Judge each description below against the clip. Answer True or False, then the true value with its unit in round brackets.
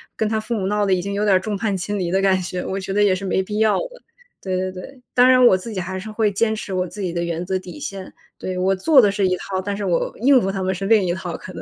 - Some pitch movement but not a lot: False (2.3 semitones)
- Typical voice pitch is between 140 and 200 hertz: True (195 Hz)